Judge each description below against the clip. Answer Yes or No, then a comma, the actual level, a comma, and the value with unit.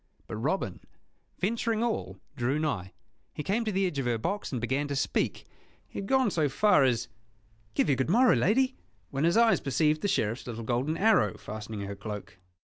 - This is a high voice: No, medium, 145 Hz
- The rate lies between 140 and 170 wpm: No, average, 195 wpm